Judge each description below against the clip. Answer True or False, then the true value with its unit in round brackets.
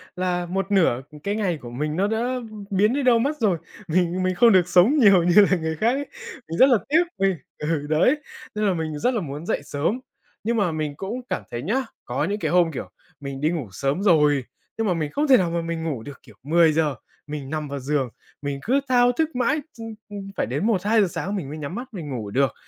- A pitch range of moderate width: False (6.3 semitones)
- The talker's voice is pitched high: False (175 Hz)